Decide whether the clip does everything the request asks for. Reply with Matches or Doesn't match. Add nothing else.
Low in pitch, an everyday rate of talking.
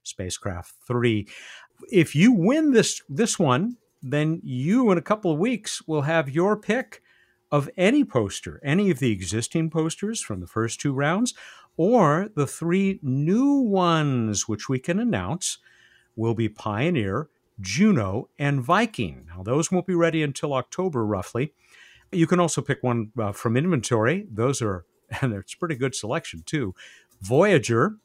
Doesn't match